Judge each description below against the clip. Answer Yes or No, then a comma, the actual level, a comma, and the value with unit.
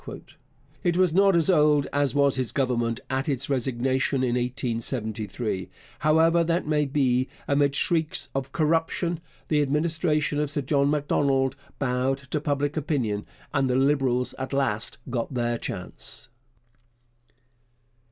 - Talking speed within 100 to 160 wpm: Yes, slow, 135 wpm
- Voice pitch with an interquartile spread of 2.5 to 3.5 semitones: Yes, average, 3.2 semitones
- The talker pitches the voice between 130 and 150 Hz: Yes, medium, 140 Hz